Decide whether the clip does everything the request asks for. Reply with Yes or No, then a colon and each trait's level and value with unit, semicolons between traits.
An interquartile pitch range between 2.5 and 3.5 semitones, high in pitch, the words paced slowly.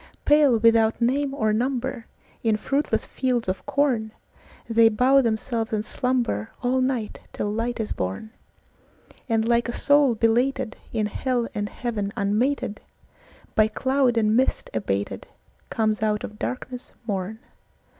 Yes: average, 3.1 semitones; high, 230 Hz; slow, 115 wpm